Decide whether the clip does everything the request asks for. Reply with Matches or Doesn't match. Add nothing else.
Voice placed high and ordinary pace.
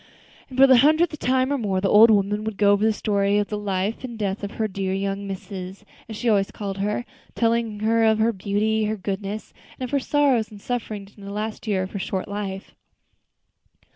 Doesn't match